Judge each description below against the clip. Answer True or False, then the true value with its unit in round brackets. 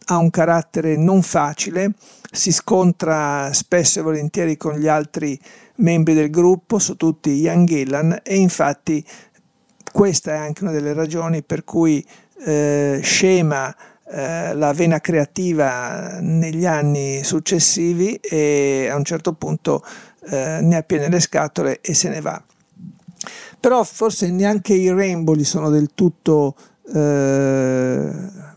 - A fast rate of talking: False (130 wpm)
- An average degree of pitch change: True (3.7 semitones)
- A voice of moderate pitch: True (165 Hz)